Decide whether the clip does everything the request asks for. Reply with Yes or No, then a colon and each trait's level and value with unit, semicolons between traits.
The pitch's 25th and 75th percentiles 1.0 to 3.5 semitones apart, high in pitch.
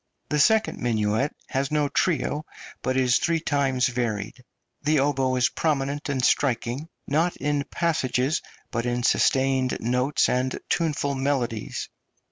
No: average, 2.7 semitones; low, 135 Hz